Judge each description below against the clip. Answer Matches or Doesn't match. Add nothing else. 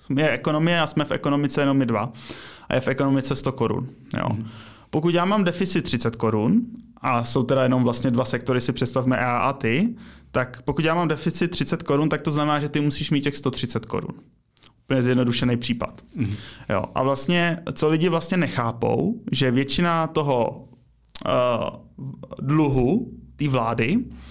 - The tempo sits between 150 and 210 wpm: Matches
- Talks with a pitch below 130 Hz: Doesn't match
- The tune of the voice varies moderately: Matches